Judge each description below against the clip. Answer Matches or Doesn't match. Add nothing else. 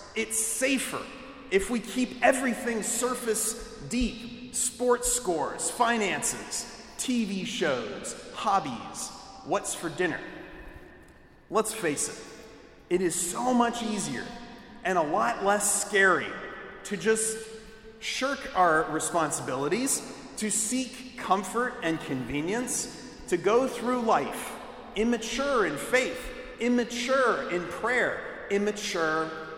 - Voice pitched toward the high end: Matches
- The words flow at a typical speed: Doesn't match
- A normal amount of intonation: Matches